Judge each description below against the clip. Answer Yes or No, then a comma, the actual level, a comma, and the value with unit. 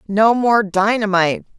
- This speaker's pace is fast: No, slow, 115 wpm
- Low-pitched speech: No, high, 210 Hz